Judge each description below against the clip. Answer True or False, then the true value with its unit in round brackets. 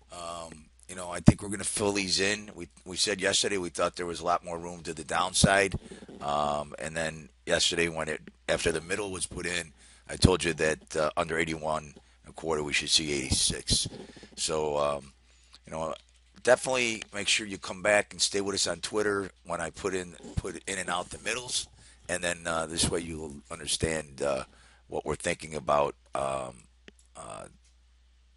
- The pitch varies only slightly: False (3.6 semitones)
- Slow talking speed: False (200 wpm)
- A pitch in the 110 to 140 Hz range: False (85 Hz)